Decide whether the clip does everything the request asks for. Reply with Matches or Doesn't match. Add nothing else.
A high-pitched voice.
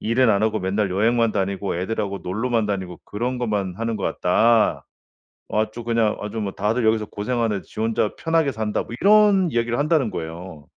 Doesn't match